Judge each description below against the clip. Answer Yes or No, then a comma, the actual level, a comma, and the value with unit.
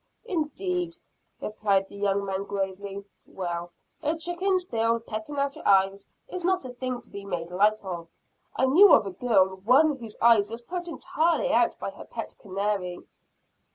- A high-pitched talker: Yes, high, 220 Hz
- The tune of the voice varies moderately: No, wide, 8.1 semitones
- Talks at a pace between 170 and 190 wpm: Yes, average, 175 wpm